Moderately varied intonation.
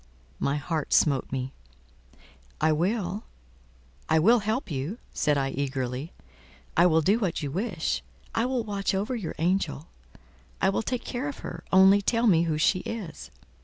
No: wide, 6.8 semitones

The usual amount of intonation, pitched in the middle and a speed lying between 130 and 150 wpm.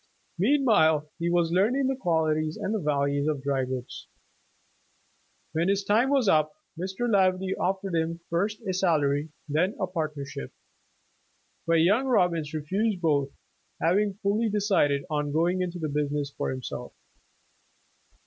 Yes: average, 4.9 semitones; medium, 170 Hz; slow, 135 wpm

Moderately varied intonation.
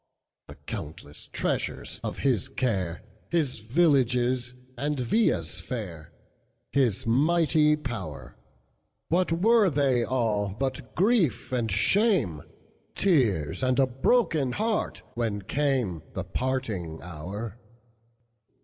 No: wide, 6.7 semitones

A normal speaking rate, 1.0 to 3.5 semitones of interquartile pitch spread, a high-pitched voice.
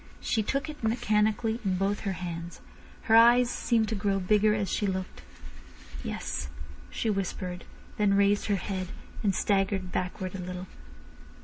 Yes: average, 150 wpm; average, 2.8 semitones; high, 200 Hz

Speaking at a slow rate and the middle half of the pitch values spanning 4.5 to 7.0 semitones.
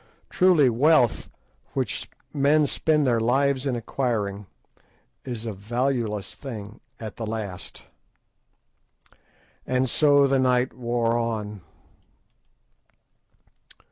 No: slow, 95 wpm; average, 3.7 semitones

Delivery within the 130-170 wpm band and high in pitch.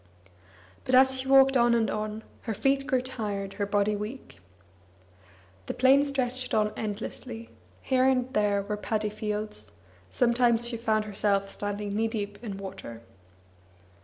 Yes: average, 145 wpm; high, 220 Hz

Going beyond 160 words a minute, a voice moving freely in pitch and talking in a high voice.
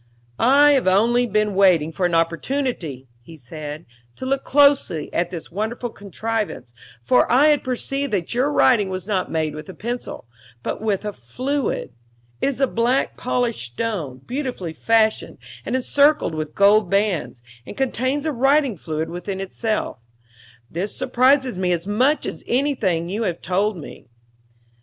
No: average, 155 wpm; wide, 7.1 semitones; high, 210 Hz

